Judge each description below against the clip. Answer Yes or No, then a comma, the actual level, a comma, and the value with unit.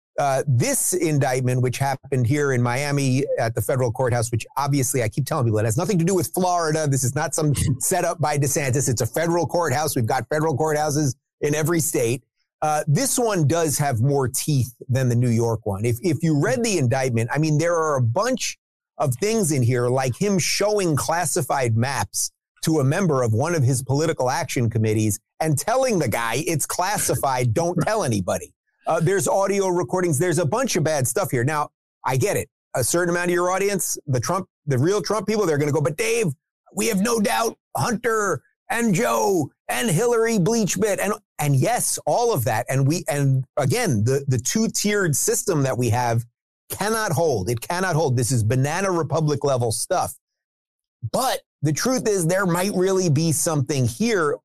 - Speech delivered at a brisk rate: No, average, 195 wpm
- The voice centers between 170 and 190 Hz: No, medium, 150 Hz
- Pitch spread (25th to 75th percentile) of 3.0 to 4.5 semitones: No, wide, 5.6 semitones